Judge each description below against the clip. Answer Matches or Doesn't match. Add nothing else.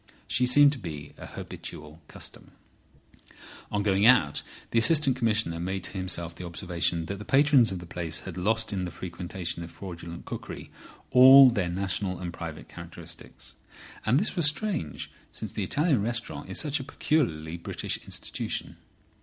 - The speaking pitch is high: Doesn't match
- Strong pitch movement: Matches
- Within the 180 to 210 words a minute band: Doesn't match